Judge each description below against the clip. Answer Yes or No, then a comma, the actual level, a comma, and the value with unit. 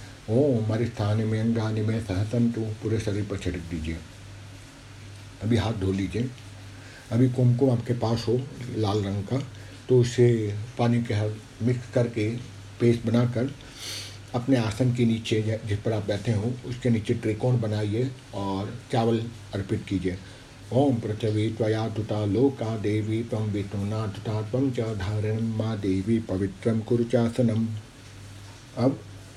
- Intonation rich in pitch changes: No, average, 2.7 semitones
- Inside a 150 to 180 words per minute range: No, average, 135 wpm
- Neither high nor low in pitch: No, low, 110 Hz